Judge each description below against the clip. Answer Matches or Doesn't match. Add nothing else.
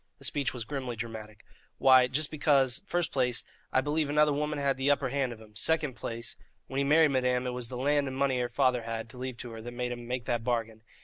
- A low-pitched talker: Matches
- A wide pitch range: Doesn't match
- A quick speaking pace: Matches